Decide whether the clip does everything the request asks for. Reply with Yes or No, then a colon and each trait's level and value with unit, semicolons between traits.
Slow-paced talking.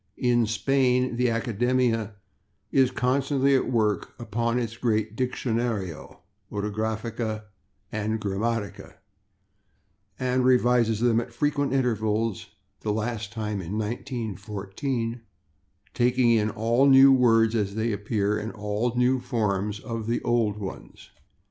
Yes: slow, 115 wpm